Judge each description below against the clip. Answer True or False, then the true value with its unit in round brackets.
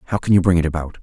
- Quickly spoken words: True (350 wpm)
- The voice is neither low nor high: False (85 Hz)